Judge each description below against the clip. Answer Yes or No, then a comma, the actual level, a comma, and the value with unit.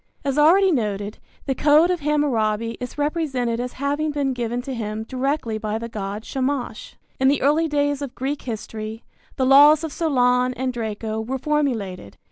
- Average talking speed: Yes, average, 170 wpm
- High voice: Yes, very high, 260 Hz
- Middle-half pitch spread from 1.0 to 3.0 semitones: No, average, 4.5 semitones